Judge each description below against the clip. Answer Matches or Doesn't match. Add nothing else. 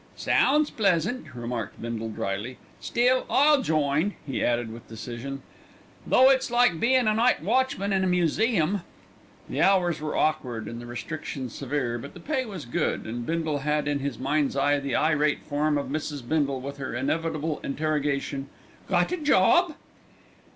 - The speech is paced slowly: Doesn't match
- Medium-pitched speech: Matches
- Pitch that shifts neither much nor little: Doesn't match